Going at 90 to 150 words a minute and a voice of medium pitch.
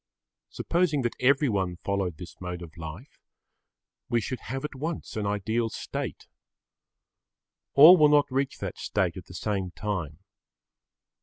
No: average, 140 wpm; low, 105 Hz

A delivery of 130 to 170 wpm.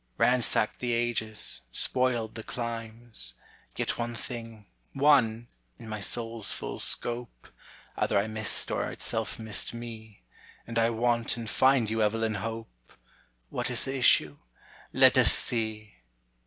Yes: slow, 135 wpm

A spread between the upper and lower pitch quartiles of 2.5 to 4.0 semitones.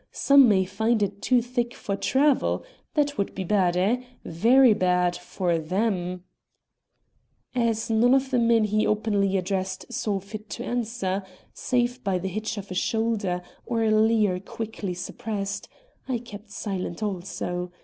Yes: average, 3.7 semitones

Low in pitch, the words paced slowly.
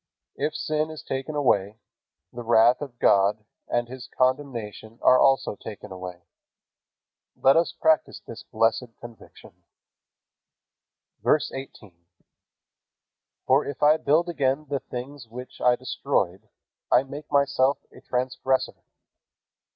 Yes: low, 130 Hz; slow, 120 wpm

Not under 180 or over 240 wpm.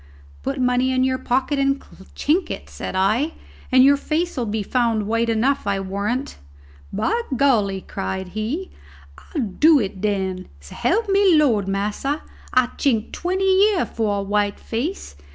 No: average, 155 wpm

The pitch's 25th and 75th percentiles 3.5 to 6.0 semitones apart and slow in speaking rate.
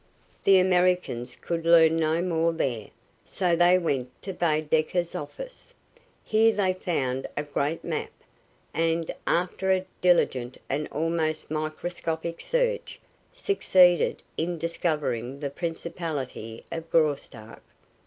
No: average, 3.0 semitones; slow, 115 wpm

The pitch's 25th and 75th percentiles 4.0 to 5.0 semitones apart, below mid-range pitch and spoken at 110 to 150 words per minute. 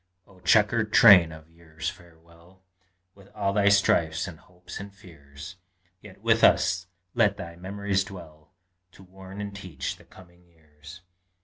No: average, 3.1 semitones; very low, 90 Hz; average, 145 wpm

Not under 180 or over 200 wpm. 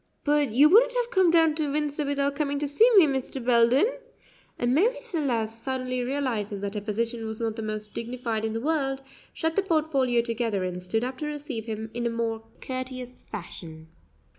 Yes: average, 190 wpm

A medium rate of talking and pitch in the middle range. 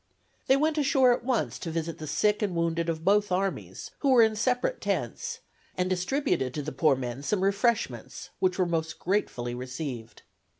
Yes: average, 180 wpm; medium, 180 Hz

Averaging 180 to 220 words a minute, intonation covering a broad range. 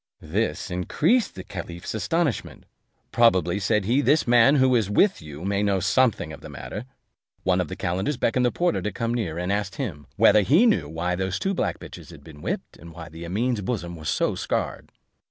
Yes: average, 200 wpm; wide, 6.0 semitones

